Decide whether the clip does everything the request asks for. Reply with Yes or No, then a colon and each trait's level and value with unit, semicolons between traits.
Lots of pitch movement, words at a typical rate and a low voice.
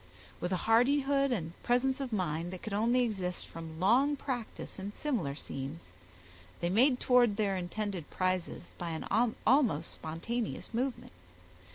No: wide, 6.0 semitones; average, 145 wpm; high, 210 Hz